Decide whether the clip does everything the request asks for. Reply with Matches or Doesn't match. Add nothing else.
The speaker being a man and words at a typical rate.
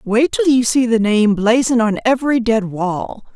Doesn't match